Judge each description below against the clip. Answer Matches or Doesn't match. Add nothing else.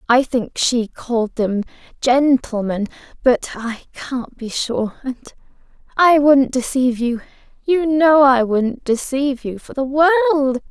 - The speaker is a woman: Matches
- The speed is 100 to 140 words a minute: Matches